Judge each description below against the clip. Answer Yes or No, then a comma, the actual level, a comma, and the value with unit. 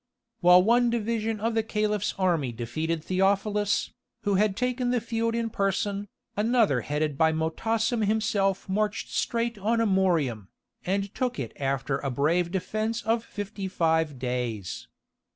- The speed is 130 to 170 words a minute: Yes, average, 140 wpm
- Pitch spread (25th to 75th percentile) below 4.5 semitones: No, wide, 5.6 semitones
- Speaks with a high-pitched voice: Yes, high, 200 Hz